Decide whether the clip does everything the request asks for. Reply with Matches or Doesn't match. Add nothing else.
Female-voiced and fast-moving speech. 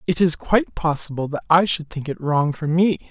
Doesn't match